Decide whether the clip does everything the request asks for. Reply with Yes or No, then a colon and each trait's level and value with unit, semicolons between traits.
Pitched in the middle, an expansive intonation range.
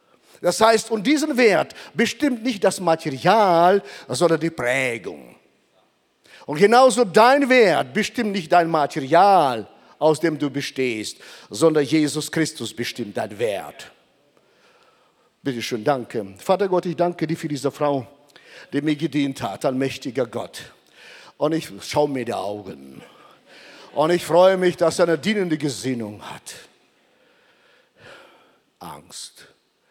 Yes: medium, 160 Hz; wide, 5.8 semitones